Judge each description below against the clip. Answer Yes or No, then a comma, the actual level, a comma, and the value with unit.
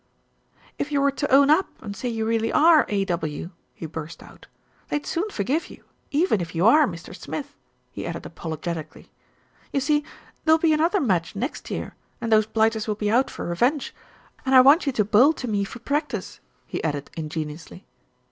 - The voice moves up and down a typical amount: No, wide, 8.1 semitones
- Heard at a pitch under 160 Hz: No, high, 225 Hz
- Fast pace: No, average, 185 wpm